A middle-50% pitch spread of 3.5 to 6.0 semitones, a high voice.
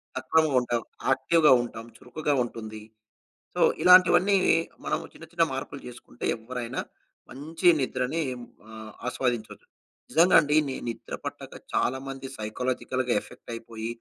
No: average, 4.8 semitones; low, 130 Hz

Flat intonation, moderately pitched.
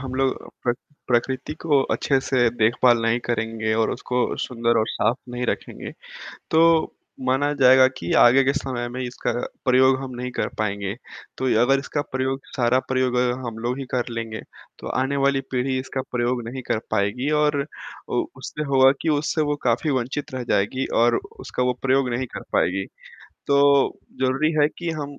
No: narrow, 2.2 semitones; low, 130 Hz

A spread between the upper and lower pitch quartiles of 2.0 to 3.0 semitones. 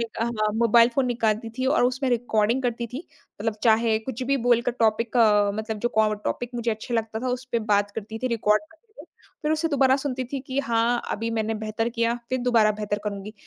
Yes: narrow, 2.5 semitones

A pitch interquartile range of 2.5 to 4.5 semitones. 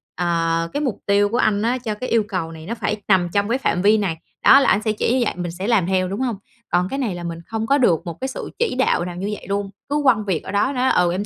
No: average, 5.0 semitones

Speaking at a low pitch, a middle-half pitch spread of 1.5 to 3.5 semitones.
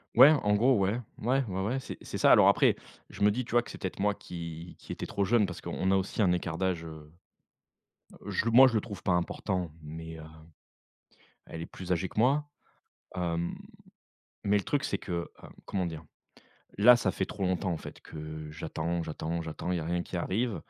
No: very low, 95 Hz; average, 4.0 semitones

